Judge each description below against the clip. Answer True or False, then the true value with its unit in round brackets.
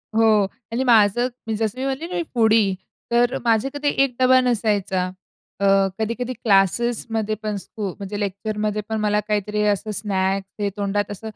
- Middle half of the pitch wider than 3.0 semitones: False (2.6 semitones)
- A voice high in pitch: True (215 Hz)